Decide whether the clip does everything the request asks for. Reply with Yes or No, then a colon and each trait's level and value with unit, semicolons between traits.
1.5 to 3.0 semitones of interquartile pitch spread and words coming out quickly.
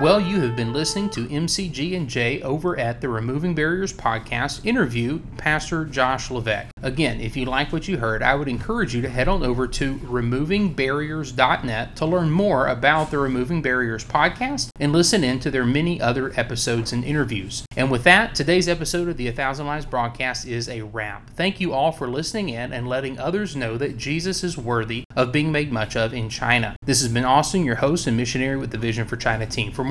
No: average, 4.7 semitones; fast, 210 wpm